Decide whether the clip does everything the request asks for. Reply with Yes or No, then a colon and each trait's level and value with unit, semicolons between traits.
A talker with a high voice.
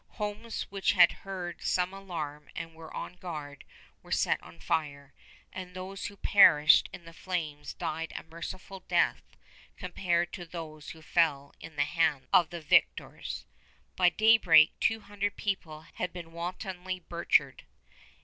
No: medium, 175 Hz